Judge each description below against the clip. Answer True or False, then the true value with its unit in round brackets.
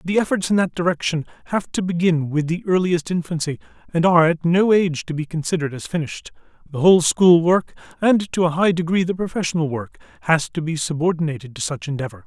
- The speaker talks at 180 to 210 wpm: True (200 wpm)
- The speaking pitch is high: False (165 Hz)